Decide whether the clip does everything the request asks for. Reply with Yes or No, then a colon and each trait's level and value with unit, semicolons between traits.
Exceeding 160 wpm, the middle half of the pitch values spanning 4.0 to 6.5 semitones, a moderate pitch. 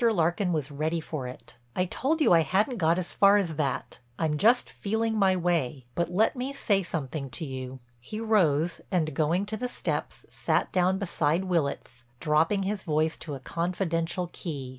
Yes: average, 185 wpm; average, 4.6 semitones; medium, 170 Hz